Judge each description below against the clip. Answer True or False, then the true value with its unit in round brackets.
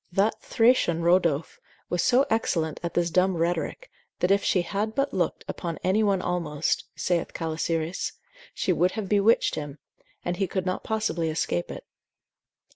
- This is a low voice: False (180 Hz)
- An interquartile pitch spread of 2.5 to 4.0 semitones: True (3.4 semitones)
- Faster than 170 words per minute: False (160 wpm)